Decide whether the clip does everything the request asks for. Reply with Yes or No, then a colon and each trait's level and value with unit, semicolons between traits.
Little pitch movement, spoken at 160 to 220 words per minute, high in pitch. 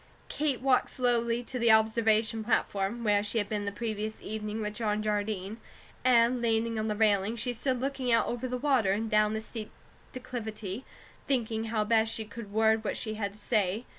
Yes: narrow, 1.9 semitones; average, 195 wpm; high, 220 Hz